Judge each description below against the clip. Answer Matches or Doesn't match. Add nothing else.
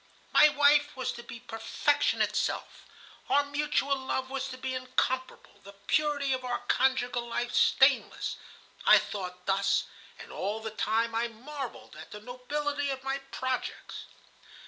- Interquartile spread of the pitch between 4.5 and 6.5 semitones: Doesn't match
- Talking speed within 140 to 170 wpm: Matches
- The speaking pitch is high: Matches